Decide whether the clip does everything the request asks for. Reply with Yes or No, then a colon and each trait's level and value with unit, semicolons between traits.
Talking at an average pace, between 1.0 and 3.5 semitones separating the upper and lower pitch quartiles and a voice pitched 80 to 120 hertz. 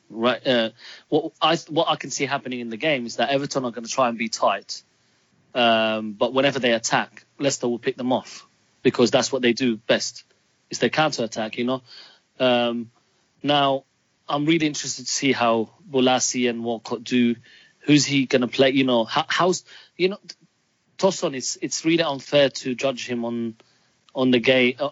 No: average, 195 wpm; average, 3.1 semitones; low, 130 Hz